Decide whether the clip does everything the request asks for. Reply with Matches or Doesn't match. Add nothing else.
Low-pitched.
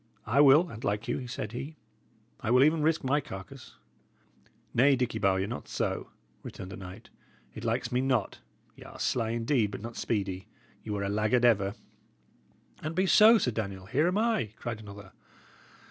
Matches